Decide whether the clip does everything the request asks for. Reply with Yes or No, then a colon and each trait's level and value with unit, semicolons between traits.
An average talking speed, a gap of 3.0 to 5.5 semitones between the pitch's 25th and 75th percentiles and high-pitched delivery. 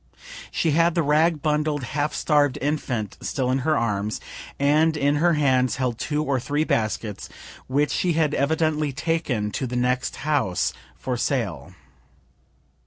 No: average, 150 wpm; average, 3.3 semitones; medium, 145 Hz